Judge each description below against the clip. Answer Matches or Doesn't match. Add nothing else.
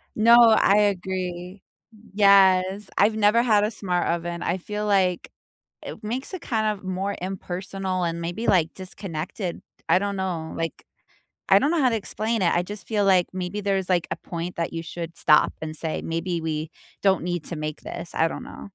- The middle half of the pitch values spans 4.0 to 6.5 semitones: Doesn't match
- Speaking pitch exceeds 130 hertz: Matches